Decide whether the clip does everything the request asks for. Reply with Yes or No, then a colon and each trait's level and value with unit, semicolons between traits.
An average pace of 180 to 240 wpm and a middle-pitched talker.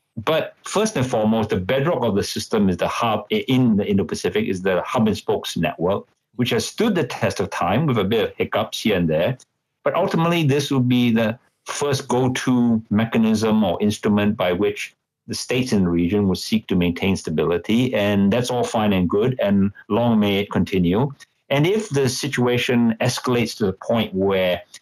No: average, 195 wpm; low, 110 Hz